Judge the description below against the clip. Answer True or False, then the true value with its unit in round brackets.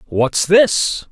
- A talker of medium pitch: True (175 Hz)